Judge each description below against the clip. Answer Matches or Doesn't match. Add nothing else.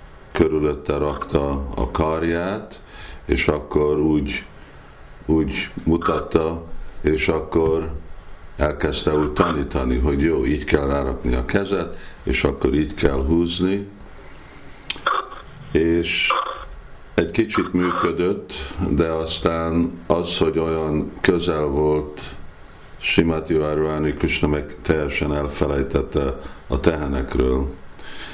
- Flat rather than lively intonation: Matches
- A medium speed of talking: Doesn't match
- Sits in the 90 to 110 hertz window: Doesn't match